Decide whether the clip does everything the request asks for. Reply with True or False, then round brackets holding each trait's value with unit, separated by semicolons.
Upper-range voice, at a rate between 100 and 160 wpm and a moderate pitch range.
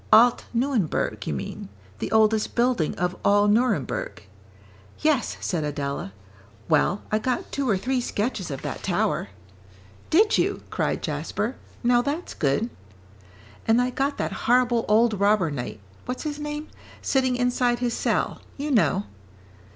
True (235 Hz; 145 wpm; 4.3 semitones)